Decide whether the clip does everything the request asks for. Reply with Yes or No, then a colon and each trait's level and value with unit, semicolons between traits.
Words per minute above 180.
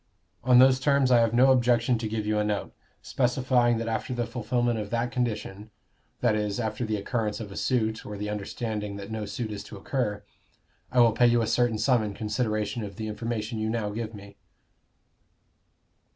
Yes: average, 195 wpm